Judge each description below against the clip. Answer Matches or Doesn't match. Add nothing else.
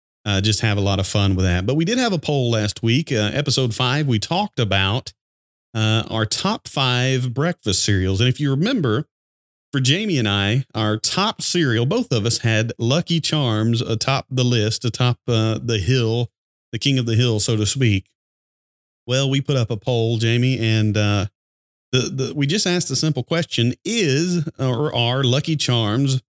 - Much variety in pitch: Doesn't match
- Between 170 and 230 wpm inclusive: Matches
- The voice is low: Matches